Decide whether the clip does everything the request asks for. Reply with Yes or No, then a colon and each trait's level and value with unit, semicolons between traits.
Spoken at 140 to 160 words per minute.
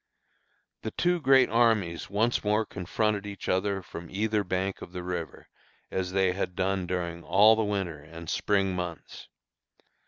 Yes: average, 155 wpm